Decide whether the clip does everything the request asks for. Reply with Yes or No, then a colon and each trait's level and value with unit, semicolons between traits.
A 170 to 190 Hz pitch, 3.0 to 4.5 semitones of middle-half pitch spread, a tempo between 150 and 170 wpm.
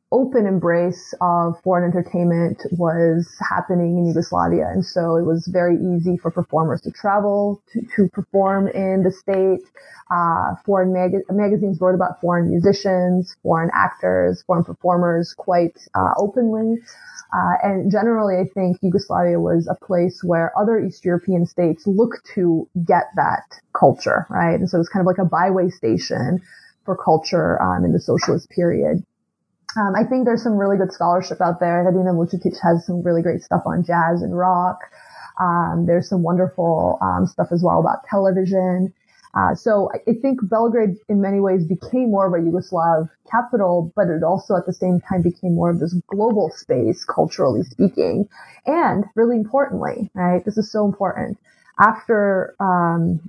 No: medium, 185 Hz; narrow, 2.6 semitones; average, 165 wpm